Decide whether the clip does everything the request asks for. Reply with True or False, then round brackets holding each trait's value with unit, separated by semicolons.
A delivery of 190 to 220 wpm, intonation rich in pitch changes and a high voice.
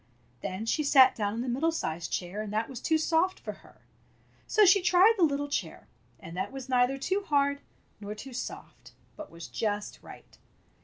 True (195 wpm; 7.0 semitones; 265 Hz)